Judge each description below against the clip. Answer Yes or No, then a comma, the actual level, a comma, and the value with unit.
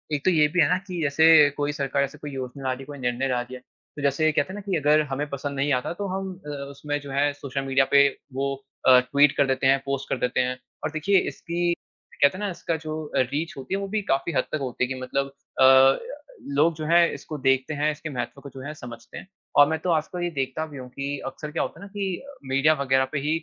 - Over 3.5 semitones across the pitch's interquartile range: No, average, 2.8 semitones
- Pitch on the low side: No, medium, 145 Hz